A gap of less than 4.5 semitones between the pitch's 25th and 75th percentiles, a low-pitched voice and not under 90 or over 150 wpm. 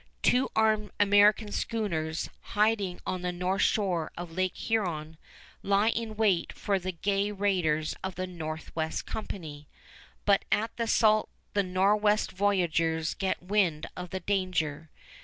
No: average, 3.7 semitones; high, 190 Hz; average, 140 wpm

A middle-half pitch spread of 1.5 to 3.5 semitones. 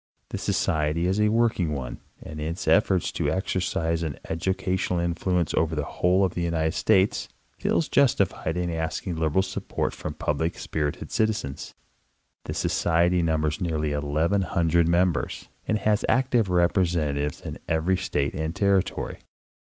Yes: average, 3.1 semitones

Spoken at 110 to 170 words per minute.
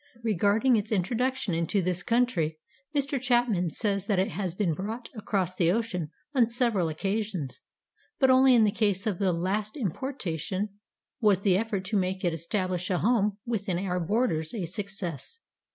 Yes: average, 165 wpm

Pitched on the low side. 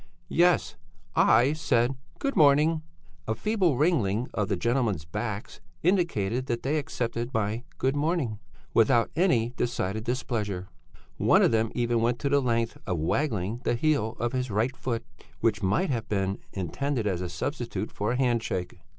Yes: low, 120 Hz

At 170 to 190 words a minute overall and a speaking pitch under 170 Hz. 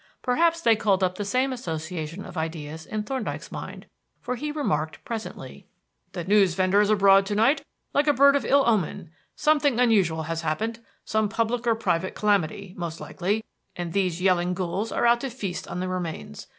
No: average, 180 wpm; high, 200 Hz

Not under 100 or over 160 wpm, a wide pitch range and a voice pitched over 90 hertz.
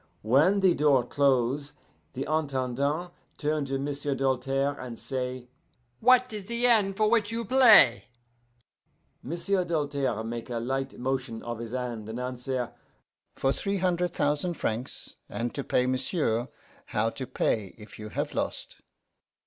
Yes: average, 145 wpm; wide, 5.8 semitones; low, 135 Hz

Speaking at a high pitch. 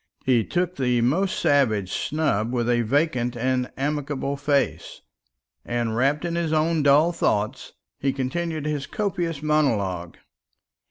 No: medium, 140 Hz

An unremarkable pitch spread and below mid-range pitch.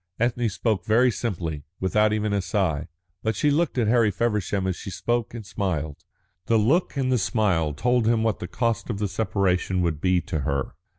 Yes: average, 4.4 semitones; low, 105 Hz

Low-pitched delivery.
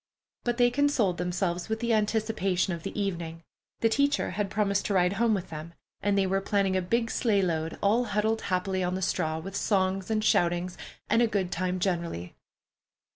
No: high, 195 Hz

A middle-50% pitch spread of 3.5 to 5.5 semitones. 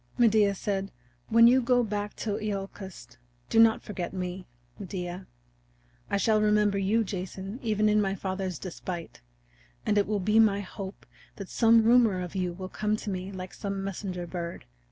No: narrow, 2.4 semitones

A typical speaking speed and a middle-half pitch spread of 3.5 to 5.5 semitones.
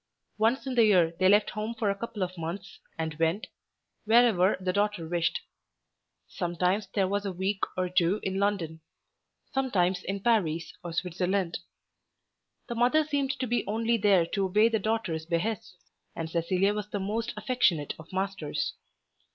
Yes: average, 160 wpm; average, 3.8 semitones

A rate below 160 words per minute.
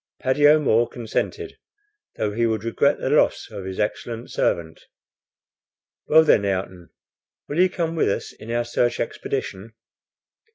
Yes: average, 140 wpm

